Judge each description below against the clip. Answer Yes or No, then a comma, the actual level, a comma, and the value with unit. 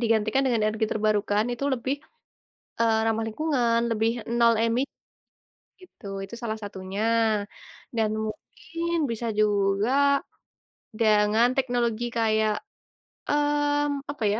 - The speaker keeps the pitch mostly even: No, average, 3.1 semitones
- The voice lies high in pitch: Yes, high, 225 Hz